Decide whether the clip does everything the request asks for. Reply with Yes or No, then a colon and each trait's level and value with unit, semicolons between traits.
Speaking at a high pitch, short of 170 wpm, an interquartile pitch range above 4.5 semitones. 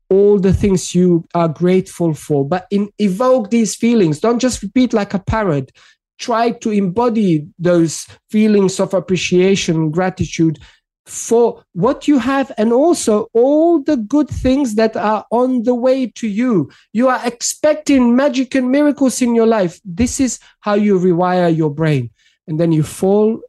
Yes: high, 215 Hz; average, 160 wpm; wide, 5.6 semitones